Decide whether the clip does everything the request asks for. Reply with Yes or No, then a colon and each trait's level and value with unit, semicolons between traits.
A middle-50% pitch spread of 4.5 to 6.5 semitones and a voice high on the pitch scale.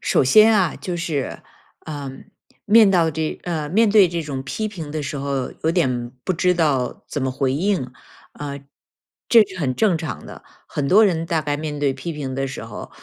No: average, 4.8 semitones; medium, 155 Hz